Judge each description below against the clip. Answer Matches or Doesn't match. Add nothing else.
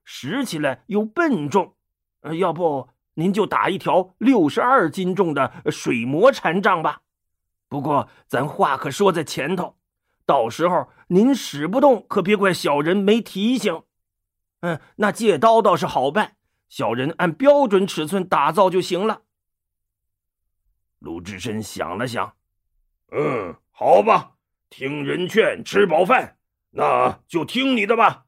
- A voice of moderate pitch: Matches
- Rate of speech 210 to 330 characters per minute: Doesn't match